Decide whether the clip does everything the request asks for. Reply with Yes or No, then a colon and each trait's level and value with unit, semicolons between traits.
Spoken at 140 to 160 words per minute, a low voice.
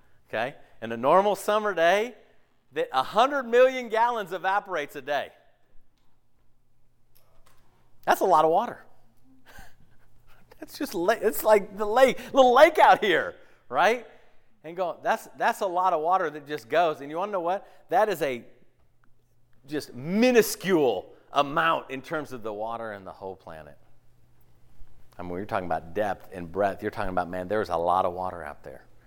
No: average, 170 wpm; low, 130 Hz